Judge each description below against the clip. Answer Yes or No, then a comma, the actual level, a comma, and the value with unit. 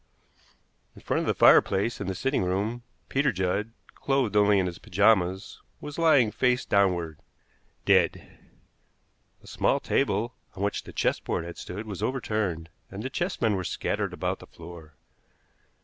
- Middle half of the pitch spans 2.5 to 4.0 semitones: No, average, 4.6 semitones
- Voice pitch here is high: No, low, 100 Hz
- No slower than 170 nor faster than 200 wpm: No, average, 150 wpm